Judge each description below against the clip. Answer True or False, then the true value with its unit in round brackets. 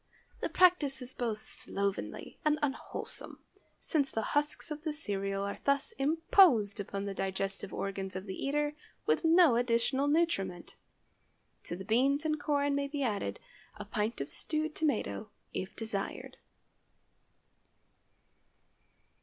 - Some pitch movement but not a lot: False (6.9 semitones)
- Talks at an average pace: False (130 wpm)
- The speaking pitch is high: True (250 Hz)